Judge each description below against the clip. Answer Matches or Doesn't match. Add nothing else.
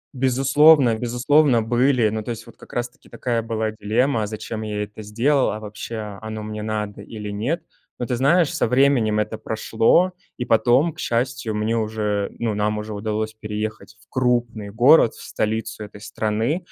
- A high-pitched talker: Doesn't match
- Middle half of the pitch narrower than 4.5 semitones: Matches